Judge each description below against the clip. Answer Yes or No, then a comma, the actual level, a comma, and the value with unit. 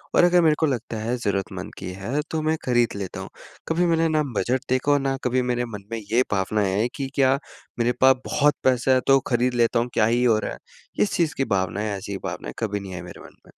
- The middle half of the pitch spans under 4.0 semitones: No, average, 4.6 semitones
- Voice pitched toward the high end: No, low, 120 Hz